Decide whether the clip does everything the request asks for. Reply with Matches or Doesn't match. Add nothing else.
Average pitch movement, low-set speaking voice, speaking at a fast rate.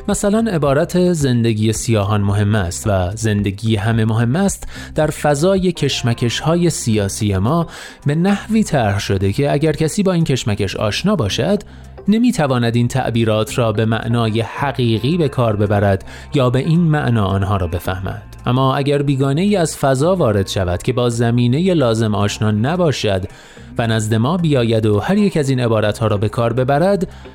Doesn't match